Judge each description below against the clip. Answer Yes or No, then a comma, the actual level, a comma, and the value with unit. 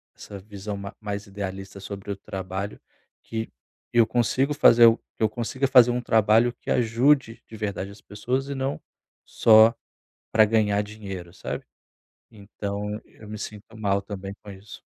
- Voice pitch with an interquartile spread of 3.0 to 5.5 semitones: No, narrow, 2.5 semitones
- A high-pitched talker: No, low, 105 Hz